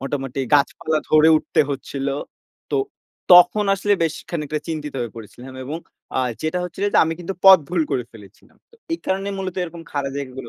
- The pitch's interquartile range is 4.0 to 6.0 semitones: Yes, average, 4.7 semitones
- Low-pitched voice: No, medium, 155 Hz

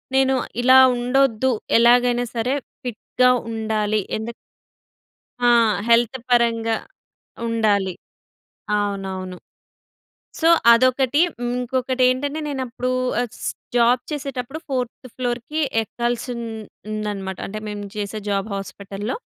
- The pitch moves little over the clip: No, average, 3.2 semitones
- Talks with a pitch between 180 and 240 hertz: Yes, high, 235 Hz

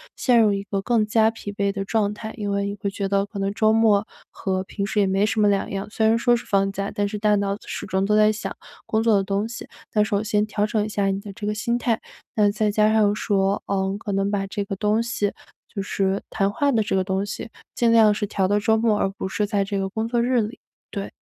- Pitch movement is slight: Yes, narrow, 1.8 semitones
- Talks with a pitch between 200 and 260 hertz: Yes, high, 205 Hz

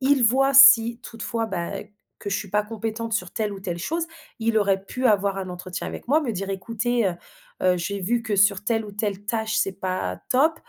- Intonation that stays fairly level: No, average, 3.3 semitones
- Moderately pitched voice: No, high, 215 Hz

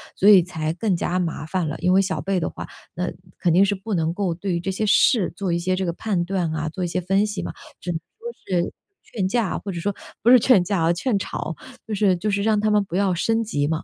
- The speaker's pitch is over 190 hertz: No, medium, 185 Hz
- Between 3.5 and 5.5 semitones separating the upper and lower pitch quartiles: No, average, 3.0 semitones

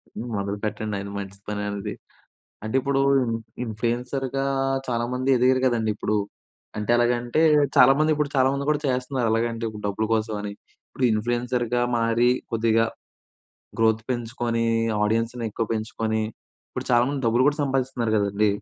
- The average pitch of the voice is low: Yes, low, 115 Hz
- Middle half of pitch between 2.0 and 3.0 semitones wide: Yes, narrow, 2.5 semitones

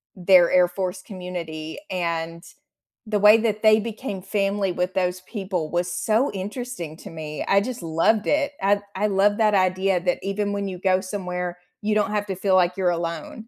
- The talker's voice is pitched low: No, high, 190 Hz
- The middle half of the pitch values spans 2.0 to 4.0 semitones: Yes, narrow, 2.6 semitones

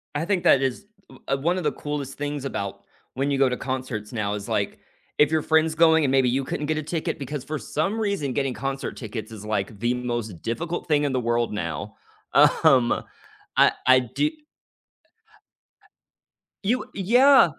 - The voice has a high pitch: No, low, 135 Hz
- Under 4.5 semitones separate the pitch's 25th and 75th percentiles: No, average, 4.8 semitones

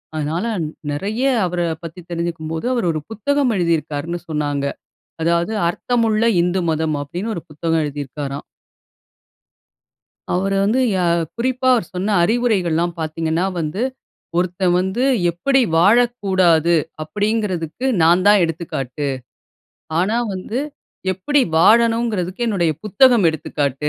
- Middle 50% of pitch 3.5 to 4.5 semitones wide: No, average, 5.3 semitones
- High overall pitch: No, medium, 175 Hz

